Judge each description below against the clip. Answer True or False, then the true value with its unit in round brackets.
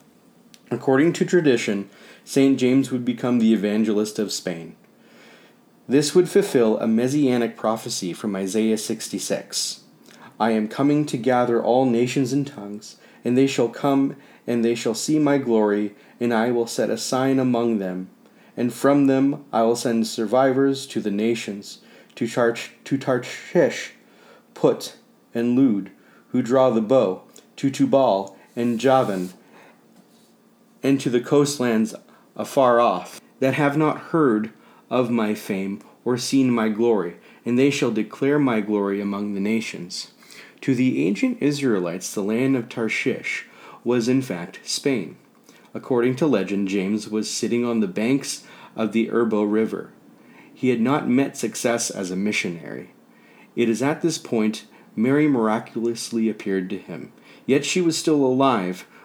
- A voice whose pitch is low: True (120 Hz)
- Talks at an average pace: True (150 wpm)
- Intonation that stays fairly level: False (3.8 semitones)